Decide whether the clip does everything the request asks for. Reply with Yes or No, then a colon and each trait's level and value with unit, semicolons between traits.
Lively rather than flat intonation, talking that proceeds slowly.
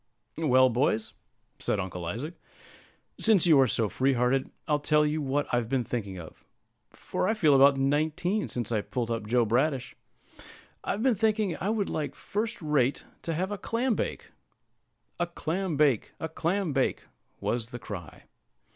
No: wide, 6.3 semitones; average, 165 wpm